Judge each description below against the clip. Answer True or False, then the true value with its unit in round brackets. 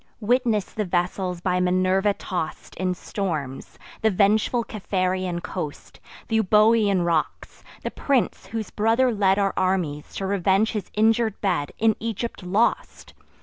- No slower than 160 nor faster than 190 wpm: False (135 wpm)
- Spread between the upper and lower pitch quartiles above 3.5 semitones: False (3.1 semitones)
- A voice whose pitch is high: True (195 Hz)